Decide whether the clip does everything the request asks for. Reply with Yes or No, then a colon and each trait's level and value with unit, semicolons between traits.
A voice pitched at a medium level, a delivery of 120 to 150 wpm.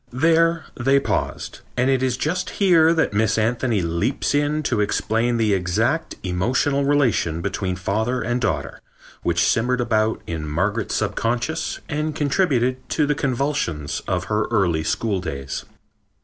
No: low, 120 Hz; average, 140 wpm